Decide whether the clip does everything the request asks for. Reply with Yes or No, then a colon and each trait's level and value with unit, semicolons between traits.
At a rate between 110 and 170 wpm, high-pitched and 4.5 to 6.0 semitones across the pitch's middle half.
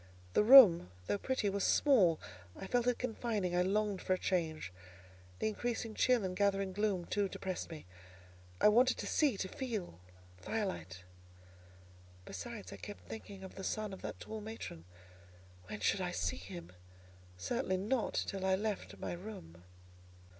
No: average, 155 wpm; high, 195 Hz; average, 4.1 semitones